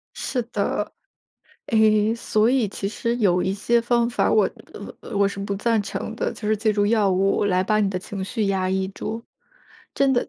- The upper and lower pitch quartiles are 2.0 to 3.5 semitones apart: Yes, average, 2.8 semitones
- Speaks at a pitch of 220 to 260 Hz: No, high, 210 Hz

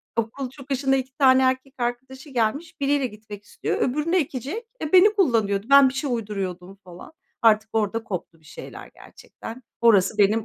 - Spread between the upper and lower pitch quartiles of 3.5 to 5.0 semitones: Yes, average, 4.4 semitones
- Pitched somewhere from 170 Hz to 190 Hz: No, very high, 250 Hz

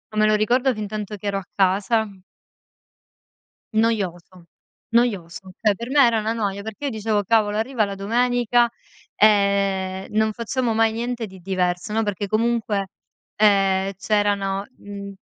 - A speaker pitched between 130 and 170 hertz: No, high, 210 Hz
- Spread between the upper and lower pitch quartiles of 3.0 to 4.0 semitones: No, narrow, 2.5 semitones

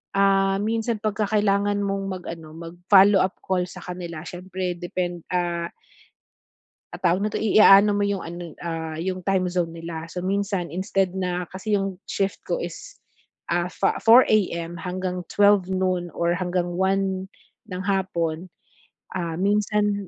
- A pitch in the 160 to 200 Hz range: Yes, medium, 185 Hz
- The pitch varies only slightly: Yes, narrow, 2.2 semitones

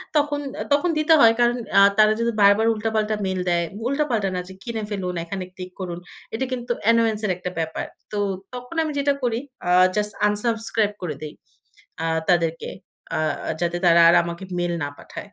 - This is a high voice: Yes, high, 210 Hz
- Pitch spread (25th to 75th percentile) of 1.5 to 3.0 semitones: No, average, 4.7 semitones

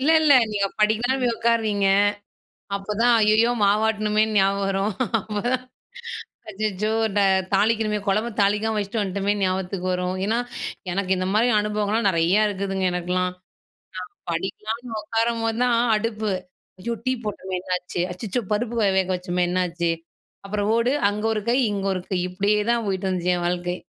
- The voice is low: No, high, 205 Hz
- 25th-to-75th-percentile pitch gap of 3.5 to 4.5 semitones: No, average, 2.8 semitones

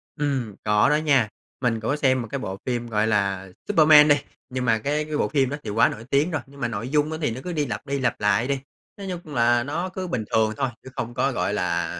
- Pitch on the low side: Yes, low, 130 Hz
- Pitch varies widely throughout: No, average, 4.7 semitones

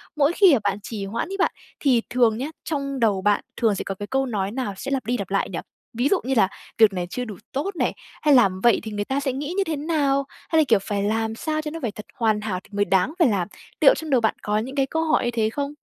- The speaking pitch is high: Yes, high, 240 Hz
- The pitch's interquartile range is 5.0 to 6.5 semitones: Yes, average, 5.3 semitones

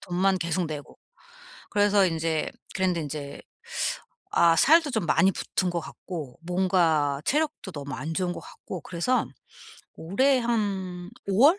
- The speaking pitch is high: No, medium, 180 Hz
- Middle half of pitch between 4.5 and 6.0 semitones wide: No, average, 3.7 semitones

